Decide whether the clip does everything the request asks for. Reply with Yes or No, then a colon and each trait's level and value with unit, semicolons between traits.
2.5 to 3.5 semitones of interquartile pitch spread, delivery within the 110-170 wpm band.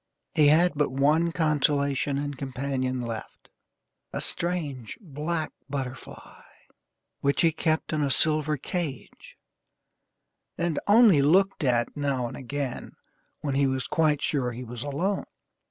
Yes: average, 3.1 semitones; slow, 135 wpm